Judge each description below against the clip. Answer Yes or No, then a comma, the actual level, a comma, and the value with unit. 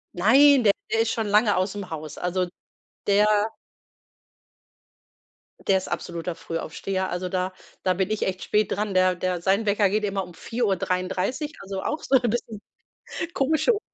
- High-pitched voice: Yes, high, 195 Hz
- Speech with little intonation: No, average, 3.2 semitones